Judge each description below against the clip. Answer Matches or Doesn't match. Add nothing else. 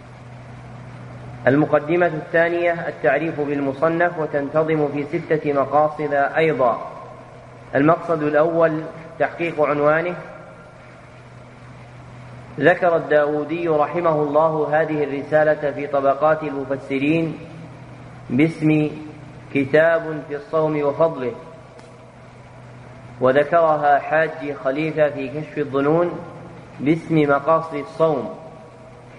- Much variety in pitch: Doesn't match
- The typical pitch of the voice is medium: Matches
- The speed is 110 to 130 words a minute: Doesn't match